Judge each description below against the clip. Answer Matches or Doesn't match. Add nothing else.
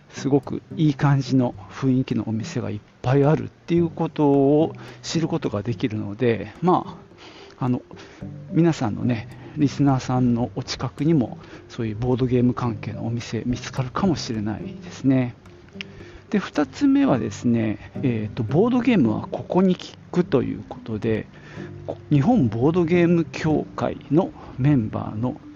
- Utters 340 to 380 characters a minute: Doesn't match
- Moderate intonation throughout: Matches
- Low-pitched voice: Matches